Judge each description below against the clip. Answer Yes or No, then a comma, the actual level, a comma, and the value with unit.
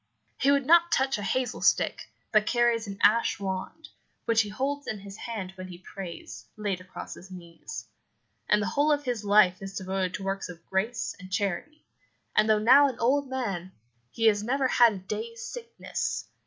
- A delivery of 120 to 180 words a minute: No, average, 190 wpm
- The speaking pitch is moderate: No, high, 215 Hz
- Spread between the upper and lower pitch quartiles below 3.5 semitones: No, wide, 5.5 semitones